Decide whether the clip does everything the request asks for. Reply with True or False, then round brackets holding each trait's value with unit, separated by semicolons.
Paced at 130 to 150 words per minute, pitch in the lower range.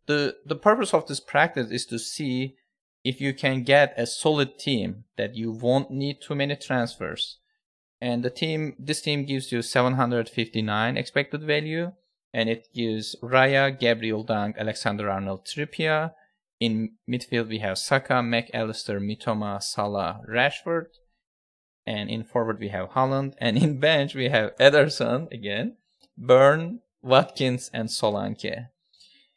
True (140 wpm; 125 Hz)